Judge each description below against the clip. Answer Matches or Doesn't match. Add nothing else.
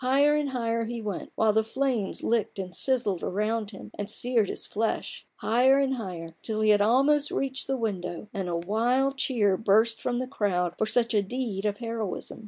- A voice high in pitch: Matches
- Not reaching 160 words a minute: Doesn't match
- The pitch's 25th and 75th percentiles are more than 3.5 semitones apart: Matches